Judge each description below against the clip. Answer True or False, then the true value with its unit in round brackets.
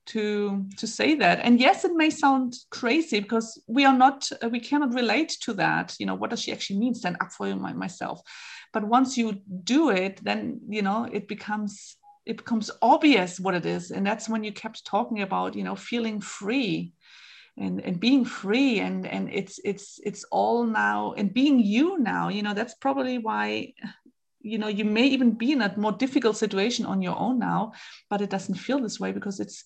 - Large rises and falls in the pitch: False (4.3 semitones)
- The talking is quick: True (210 wpm)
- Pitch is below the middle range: False (220 Hz)